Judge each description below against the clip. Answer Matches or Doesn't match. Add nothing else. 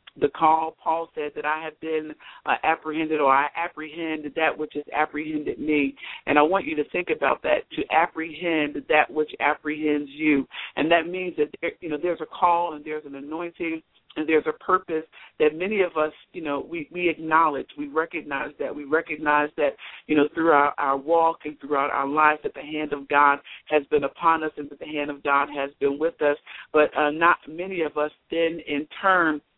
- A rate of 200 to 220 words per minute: Matches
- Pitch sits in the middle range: Matches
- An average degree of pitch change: Doesn't match